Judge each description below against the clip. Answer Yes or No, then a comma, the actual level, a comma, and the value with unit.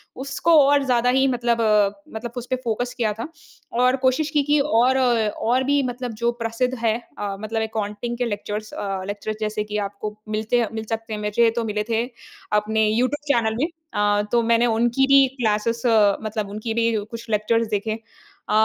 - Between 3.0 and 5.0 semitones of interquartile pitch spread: No, narrow, 2.6 semitones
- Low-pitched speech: No, high, 230 Hz